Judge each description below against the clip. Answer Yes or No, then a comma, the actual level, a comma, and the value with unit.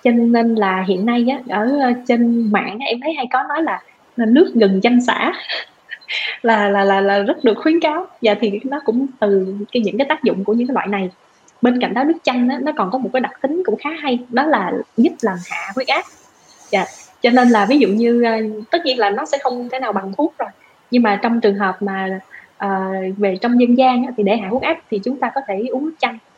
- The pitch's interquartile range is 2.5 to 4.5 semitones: Yes, average, 4.0 semitones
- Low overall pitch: No, high, 240 Hz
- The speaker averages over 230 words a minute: Yes, average, 245 wpm